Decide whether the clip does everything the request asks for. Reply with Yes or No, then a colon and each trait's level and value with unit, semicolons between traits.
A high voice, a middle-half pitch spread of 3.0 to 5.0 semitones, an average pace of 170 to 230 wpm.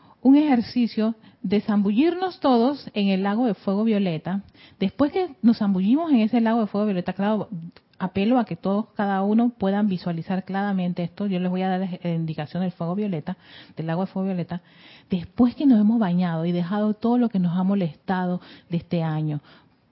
Yes: high, 195 Hz; average, 3.8 semitones; fast, 190 wpm